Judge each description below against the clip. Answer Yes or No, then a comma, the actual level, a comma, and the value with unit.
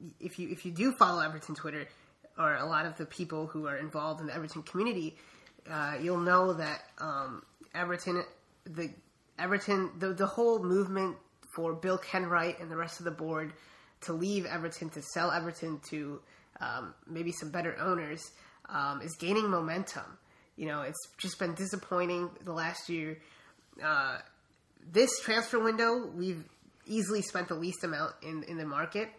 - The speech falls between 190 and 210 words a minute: No, average, 165 wpm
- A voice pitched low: No, medium, 170 Hz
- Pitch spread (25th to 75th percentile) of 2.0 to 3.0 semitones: Yes, average, 2.7 semitones